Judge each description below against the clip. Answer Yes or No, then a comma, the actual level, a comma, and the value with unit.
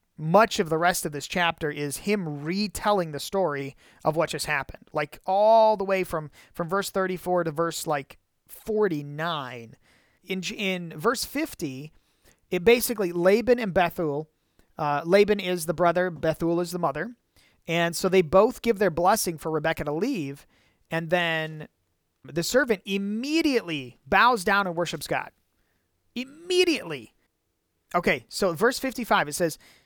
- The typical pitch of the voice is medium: Yes, medium, 175 Hz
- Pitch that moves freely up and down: No, average, 4.8 semitones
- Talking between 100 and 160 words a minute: Yes, average, 150 wpm